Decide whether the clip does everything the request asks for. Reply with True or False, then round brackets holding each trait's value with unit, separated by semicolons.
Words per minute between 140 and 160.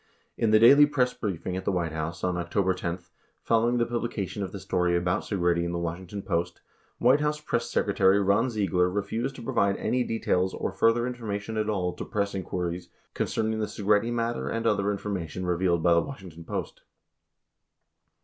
False (185 wpm)